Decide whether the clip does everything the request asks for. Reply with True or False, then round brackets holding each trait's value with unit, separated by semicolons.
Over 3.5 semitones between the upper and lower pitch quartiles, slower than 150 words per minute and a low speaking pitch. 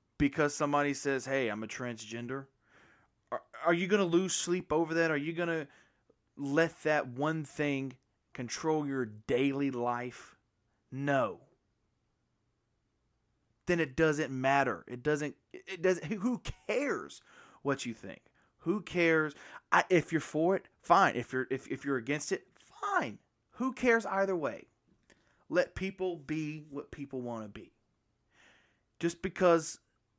False (5.2 semitones; 140 wpm; 145 Hz)